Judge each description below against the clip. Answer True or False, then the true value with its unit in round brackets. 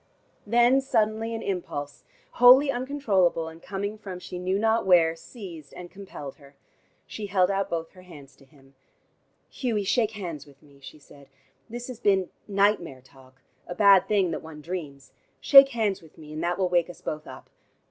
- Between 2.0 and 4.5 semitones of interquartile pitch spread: False (5.6 semitones)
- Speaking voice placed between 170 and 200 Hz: True (185 Hz)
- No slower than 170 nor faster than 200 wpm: True (180 wpm)